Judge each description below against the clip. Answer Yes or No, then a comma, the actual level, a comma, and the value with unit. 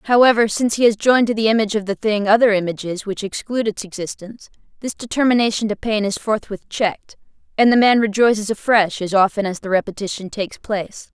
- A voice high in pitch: Yes, high, 215 Hz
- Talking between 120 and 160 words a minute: No, average, 195 wpm